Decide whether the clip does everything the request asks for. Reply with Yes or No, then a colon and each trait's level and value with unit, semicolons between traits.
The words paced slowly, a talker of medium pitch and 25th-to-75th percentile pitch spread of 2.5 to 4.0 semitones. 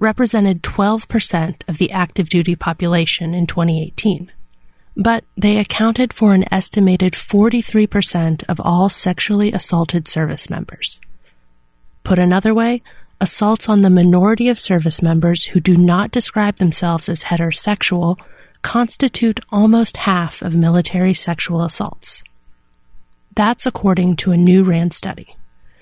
Yes: slow, 125 wpm; medium, 180 Hz; average, 3.6 semitones